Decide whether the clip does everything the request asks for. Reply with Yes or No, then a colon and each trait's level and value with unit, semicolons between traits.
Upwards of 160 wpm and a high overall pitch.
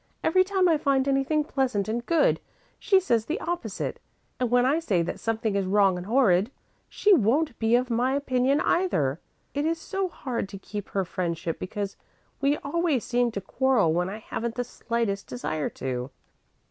Yes: average, 180 wpm; high, 245 Hz